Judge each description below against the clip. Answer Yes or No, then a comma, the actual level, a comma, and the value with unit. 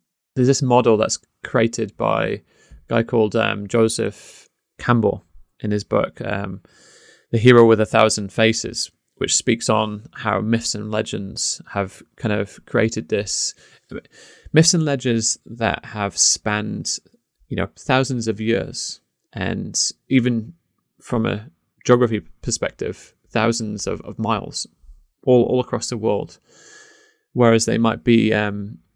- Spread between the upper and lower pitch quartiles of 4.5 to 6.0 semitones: No, average, 2.7 semitones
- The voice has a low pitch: Yes, low, 115 Hz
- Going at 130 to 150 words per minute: Yes, slow, 135 wpm